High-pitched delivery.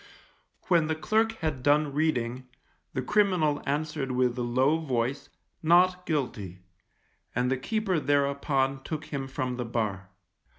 No: medium, 140 Hz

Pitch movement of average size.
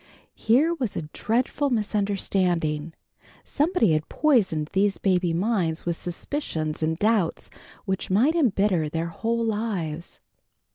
No: wide, 5.8 semitones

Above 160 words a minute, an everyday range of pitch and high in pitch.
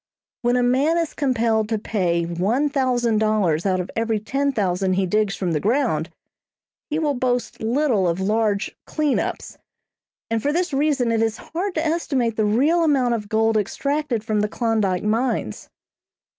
Yes: average, 170 wpm; average, 4.8 semitones; high, 225 Hz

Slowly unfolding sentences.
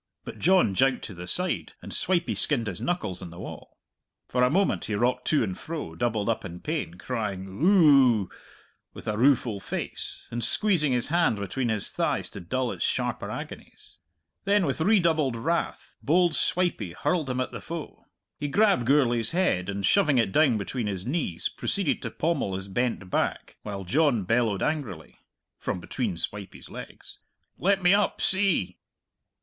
No: average, 170 wpm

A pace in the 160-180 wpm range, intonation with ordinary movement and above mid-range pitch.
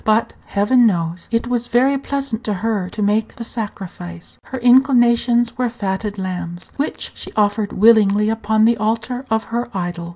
Yes: average, 165 wpm; average, 3.2 semitones; high, 220 Hz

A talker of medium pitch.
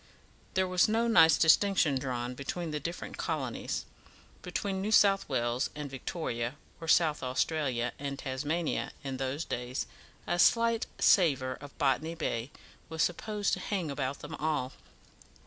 Yes: medium, 150 Hz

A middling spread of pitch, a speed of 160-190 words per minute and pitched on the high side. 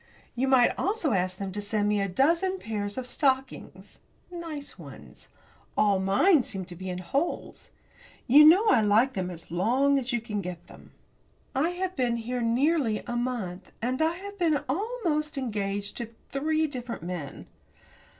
No: wide, 7.0 semitones; average, 170 wpm; very high, 250 Hz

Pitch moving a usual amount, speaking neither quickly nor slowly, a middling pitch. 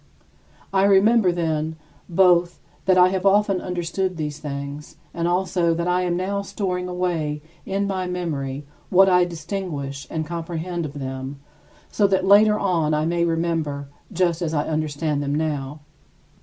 Yes: average, 3.4 semitones; average, 155 wpm; medium, 170 Hz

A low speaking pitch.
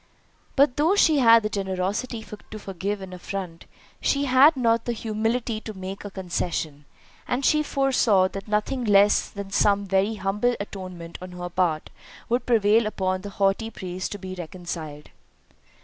No: high, 200 Hz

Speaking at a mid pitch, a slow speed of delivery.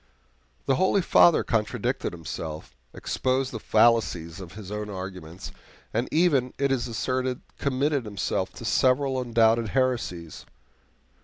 No: low, 120 Hz; slow, 125 wpm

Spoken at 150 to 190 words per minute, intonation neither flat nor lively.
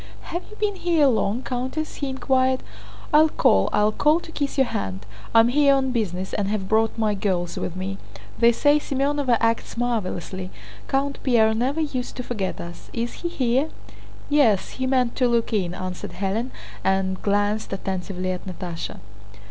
No: average, 170 wpm; wide, 5.8 semitones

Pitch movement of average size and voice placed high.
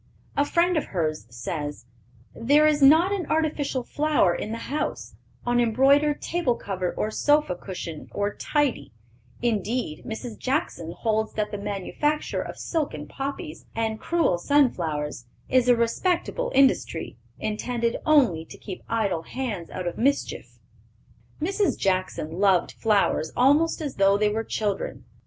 No: wide, 7.4 semitones; high, 230 Hz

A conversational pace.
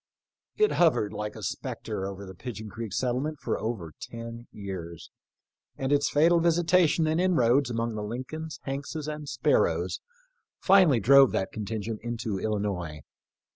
Yes: average, 150 wpm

